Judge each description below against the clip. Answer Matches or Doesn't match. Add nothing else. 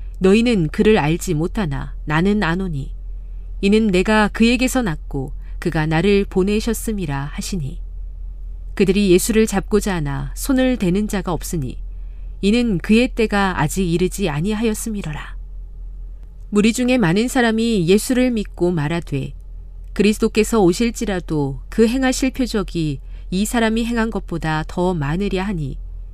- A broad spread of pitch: Matches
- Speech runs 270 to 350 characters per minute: Matches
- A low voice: Doesn't match